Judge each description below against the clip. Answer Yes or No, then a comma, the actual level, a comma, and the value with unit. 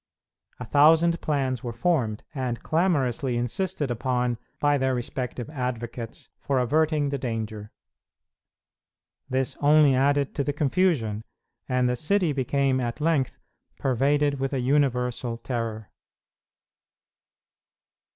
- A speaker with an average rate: No, slow, 110 wpm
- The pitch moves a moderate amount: Yes, average, 3.2 semitones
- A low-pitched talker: Yes, low, 130 Hz